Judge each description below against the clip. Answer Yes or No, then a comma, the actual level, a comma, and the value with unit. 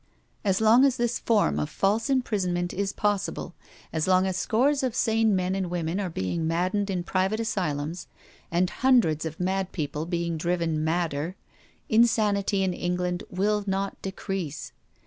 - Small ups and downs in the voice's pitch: No, average, 3.5 semitones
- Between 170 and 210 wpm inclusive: No, average, 155 wpm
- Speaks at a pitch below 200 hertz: Yes, medium, 185 Hz